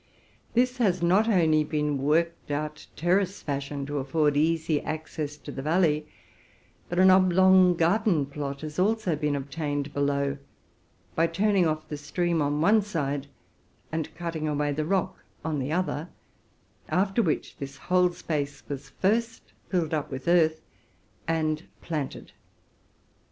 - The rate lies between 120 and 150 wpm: Yes, average, 145 wpm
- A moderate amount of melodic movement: Yes, average, 3.6 semitones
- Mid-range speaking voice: Yes, medium, 155 Hz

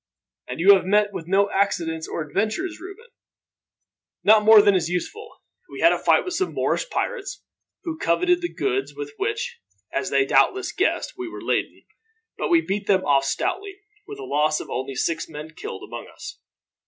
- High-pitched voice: Yes, high, 215 Hz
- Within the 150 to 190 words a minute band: Yes, average, 185 wpm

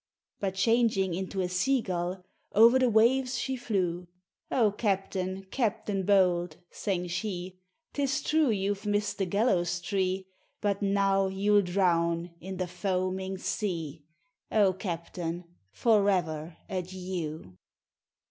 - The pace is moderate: No, slow, 120 wpm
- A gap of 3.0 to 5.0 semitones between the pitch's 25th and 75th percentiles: No, narrow, 2.6 semitones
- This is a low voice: No, high, 190 Hz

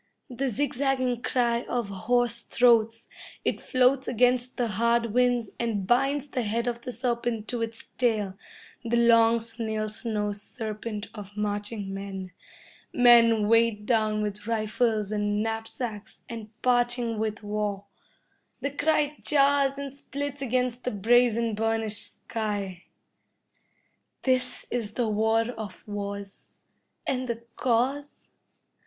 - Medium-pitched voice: No, high, 230 Hz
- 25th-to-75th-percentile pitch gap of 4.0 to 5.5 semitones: No, narrow, 2.6 semitones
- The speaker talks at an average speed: No, slow, 125 wpm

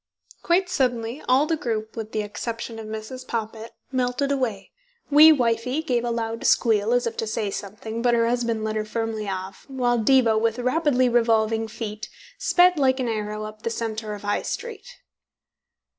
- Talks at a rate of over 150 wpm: Yes, average, 180 wpm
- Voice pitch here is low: No, high, 230 Hz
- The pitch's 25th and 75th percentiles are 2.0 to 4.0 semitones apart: Yes, average, 2.7 semitones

